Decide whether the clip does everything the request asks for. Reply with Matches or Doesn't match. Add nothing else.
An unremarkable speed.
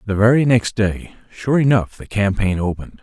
Matches